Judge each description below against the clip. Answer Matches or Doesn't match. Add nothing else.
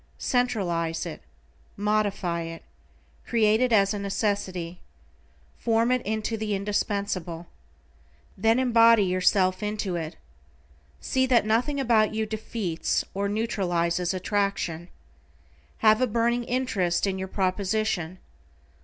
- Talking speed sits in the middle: Doesn't match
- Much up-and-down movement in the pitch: Doesn't match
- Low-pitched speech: Doesn't match